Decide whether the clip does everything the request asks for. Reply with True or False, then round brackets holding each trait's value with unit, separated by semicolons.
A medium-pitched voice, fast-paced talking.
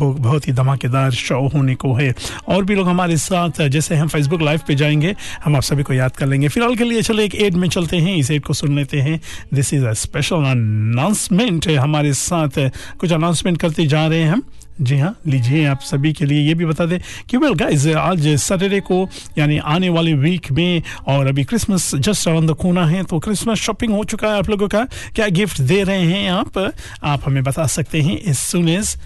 True (160 Hz; 220 wpm)